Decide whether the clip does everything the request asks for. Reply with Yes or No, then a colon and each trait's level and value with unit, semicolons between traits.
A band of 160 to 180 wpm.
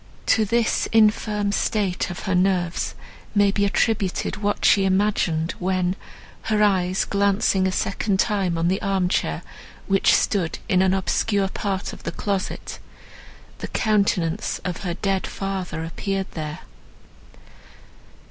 No: slow, 135 wpm